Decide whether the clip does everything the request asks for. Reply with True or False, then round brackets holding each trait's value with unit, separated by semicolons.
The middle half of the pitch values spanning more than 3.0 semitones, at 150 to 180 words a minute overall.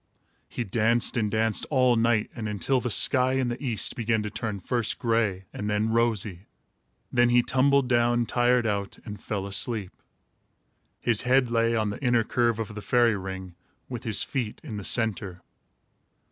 False (2.6 semitones; 175 wpm)